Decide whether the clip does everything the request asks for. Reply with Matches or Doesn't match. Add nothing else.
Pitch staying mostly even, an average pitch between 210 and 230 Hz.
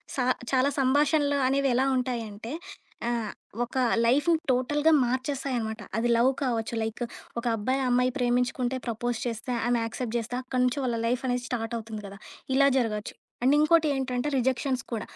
Doesn't match